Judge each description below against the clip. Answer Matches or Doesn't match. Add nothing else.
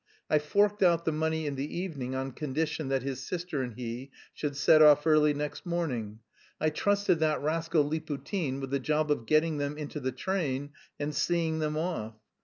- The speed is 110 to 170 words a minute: Doesn't match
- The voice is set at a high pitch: Doesn't match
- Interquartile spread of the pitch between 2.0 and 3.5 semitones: Matches